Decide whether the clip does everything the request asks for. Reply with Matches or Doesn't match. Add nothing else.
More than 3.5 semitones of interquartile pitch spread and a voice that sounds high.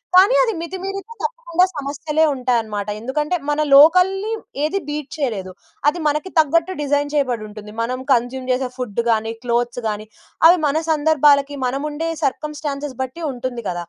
Matches